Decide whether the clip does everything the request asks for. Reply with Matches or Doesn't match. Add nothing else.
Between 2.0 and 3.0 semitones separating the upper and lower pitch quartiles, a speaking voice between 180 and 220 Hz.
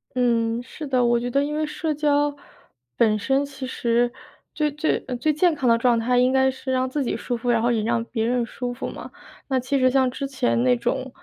Doesn't match